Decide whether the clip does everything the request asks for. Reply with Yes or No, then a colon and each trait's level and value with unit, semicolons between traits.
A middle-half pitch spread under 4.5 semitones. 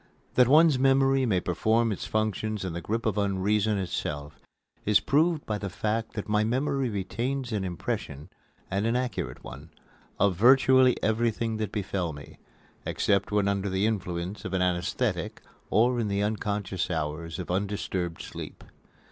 Yes: average, 3.8 semitones